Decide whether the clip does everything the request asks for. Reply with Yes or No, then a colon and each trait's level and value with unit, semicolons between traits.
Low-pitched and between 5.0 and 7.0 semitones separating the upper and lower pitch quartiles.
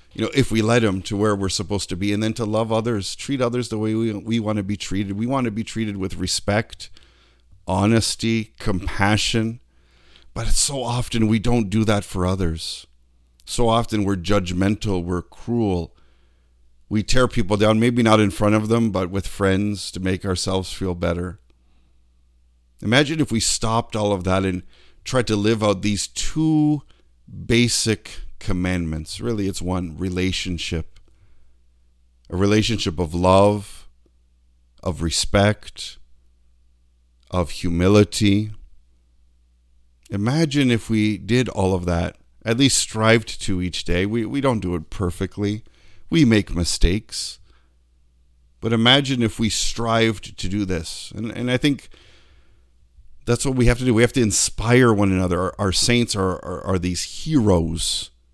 Yes: low, 100 Hz; average, 5.3 semitones